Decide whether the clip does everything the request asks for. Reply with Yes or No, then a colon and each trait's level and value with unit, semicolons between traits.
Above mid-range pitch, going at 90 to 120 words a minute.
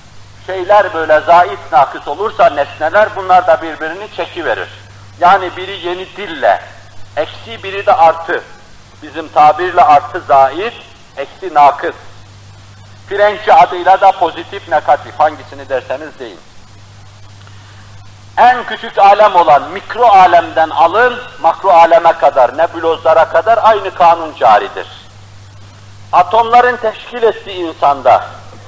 No: medium, 160 Hz; average, 110 wpm